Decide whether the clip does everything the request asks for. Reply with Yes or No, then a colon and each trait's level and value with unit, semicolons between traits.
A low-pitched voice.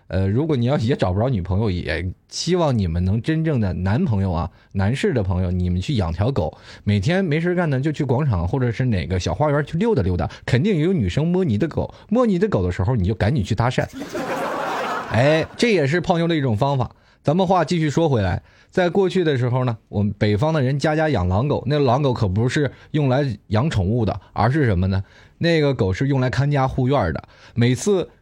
Yes: low, 120 Hz